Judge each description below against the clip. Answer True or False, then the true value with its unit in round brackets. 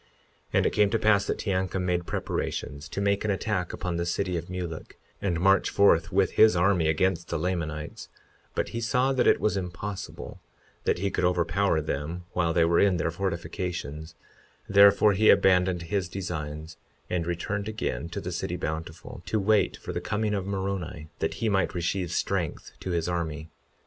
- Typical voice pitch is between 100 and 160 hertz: False (90 Hz)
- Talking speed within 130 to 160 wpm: False (185 wpm)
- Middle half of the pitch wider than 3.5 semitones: False (3.1 semitones)